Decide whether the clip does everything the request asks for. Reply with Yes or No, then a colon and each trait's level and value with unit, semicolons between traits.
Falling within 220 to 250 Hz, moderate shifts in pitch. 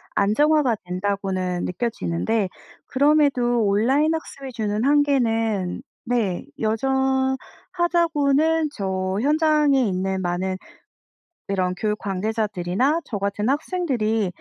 No: high, 225 Hz; wide, 6.4 semitones